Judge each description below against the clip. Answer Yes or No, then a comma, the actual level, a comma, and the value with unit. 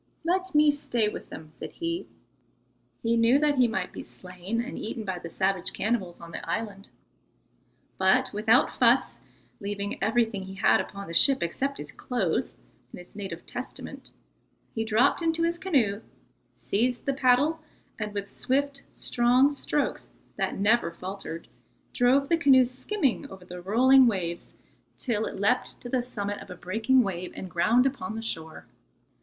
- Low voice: No, high, 225 Hz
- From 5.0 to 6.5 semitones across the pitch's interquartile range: Yes, wide, 5.6 semitones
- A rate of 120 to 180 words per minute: Yes, average, 160 wpm